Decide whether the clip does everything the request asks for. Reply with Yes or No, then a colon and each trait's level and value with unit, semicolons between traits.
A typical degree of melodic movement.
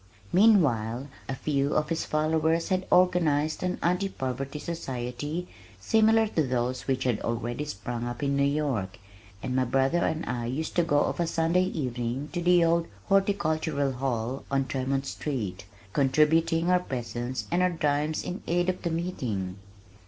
Yes: average, 5.0 semitones